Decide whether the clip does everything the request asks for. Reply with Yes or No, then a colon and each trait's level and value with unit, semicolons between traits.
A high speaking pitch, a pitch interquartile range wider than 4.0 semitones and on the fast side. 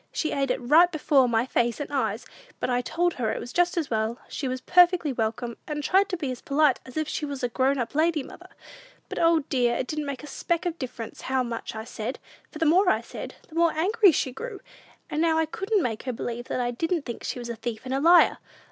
Yes: very high, 275 Hz; average, 5.3 semitones; fast, 245 wpm